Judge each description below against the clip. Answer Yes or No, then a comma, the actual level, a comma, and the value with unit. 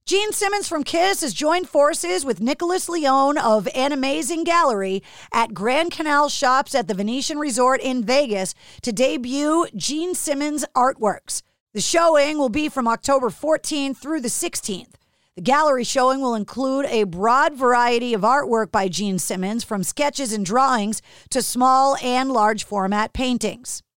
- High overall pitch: Yes, very high, 265 Hz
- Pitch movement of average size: Yes, average, 4.7 semitones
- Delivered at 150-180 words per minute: Yes, average, 155 wpm